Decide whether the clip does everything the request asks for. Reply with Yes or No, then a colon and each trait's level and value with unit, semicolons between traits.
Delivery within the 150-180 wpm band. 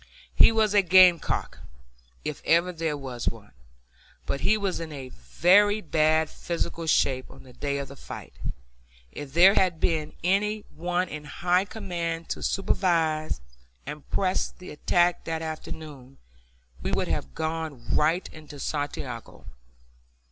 No: average, 140 wpm